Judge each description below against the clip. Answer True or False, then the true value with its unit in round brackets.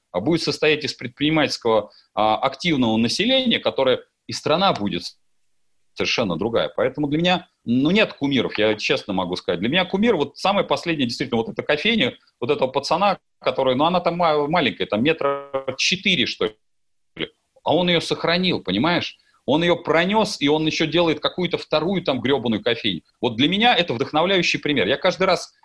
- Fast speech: True (170 wpm)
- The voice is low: False (155 Hz)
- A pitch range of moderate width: True (5.0 semitones)